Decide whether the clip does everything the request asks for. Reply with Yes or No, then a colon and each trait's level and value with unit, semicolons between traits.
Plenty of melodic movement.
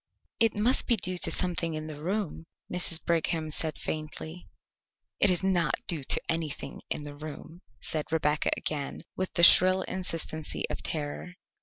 No: average, 2.9 semitones